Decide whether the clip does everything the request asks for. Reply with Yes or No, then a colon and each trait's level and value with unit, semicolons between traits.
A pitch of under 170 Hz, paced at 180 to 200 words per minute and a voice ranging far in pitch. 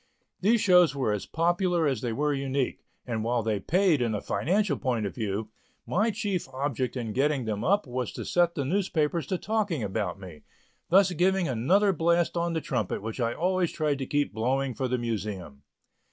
Yes: medium, 140 Hz; average, 195 wpm; wide, 7.3 semitones